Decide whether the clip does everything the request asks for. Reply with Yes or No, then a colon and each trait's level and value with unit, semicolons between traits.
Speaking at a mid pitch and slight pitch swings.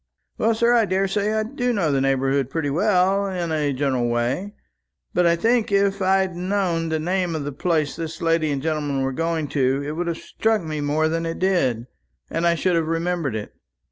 No: medium, 165 Hz; average, 4.8 semitones